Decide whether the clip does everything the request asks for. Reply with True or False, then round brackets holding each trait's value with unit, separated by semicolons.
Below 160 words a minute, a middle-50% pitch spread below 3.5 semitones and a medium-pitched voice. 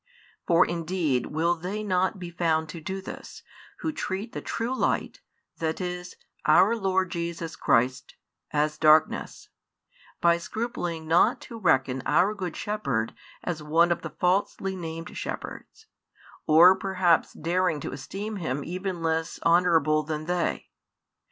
True (140 wpm; 3.0 semitones; 170 Hz)